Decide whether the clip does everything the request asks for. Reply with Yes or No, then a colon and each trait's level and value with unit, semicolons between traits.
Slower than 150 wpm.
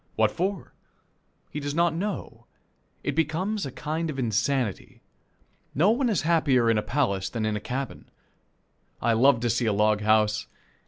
No: average, 165 wpm